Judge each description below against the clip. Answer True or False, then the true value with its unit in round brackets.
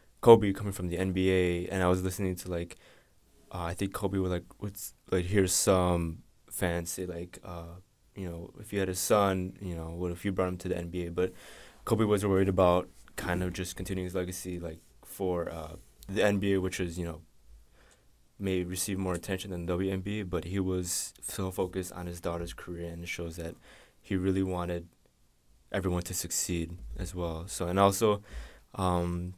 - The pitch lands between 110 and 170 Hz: False (90 Hz)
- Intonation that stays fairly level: True (1.7 semitones)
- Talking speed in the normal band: True (195 wpm)